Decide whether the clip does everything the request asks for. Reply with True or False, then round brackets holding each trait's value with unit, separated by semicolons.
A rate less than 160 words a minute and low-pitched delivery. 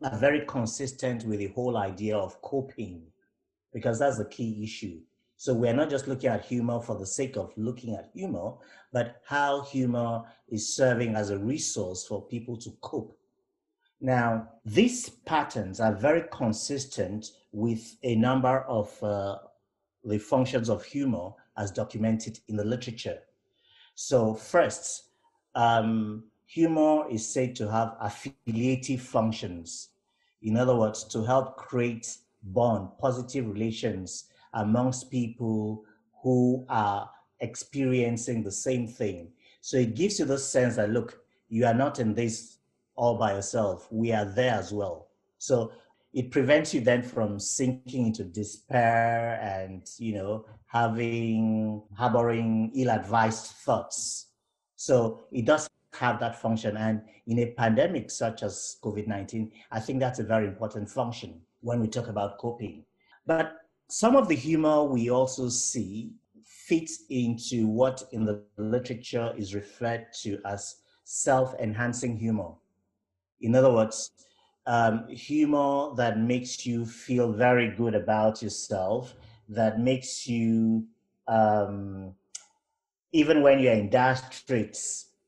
True (135 wpm; 115 Hz)